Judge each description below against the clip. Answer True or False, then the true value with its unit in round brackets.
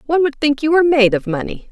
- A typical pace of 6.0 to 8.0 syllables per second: True (7.0 syllables/s)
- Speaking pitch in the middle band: False (275 Hz)